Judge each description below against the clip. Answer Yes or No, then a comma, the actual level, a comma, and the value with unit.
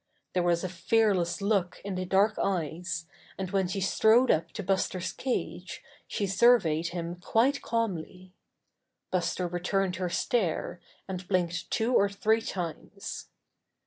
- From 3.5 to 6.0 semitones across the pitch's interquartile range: No, average, 2.7 semitones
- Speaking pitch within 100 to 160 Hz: No, medium, 185 Hz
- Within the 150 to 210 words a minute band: No, average, 140 wpm